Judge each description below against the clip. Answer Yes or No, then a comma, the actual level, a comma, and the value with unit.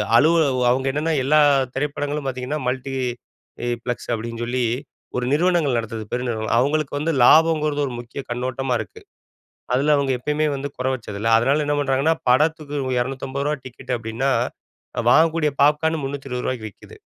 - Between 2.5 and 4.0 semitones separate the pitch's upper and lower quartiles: Yes, average, 3.3 semitones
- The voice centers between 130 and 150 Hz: Yes, low, 135 Hz